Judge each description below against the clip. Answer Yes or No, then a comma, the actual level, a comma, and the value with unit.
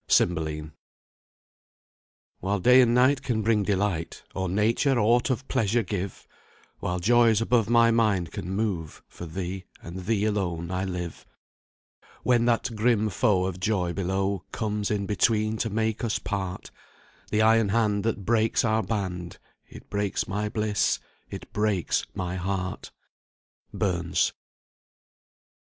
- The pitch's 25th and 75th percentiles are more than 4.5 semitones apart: No, average, 3.3 semitones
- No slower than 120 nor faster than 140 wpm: Yes, slow, 135 wpm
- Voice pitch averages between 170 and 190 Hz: No, low, 105 Hz